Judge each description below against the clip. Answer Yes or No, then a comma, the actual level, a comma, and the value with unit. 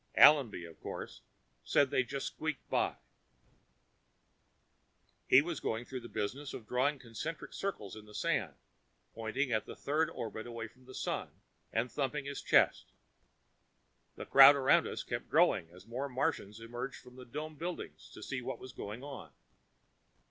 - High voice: No, low, 130 Hz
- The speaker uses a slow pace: No, average, 160 wpm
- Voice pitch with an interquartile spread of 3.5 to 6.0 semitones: Yes, average, 3.8 semitones